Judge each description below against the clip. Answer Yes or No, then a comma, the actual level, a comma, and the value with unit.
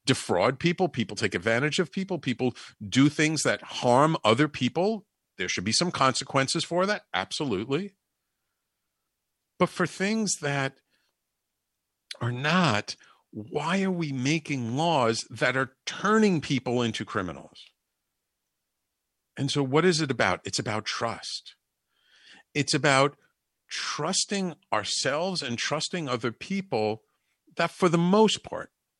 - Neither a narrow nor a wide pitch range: No, wide, 6.7 semitones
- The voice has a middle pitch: Yes, medium, 145 Hz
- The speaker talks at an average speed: No, slow, 125 wpm